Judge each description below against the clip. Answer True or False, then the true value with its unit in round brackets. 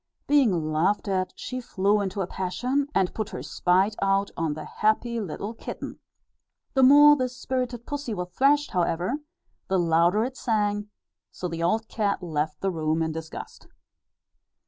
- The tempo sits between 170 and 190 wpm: False (160 wpm)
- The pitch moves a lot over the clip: True (5.7 semitones)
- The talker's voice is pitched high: True (200 Hz)